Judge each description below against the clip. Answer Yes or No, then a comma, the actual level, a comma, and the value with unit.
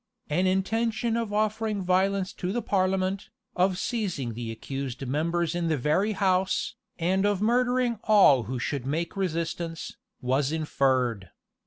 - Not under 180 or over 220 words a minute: No, average, 140 wpm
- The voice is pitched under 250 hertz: Yes, medium, 185 Hz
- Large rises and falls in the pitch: Yes, wide, 5.8 semitones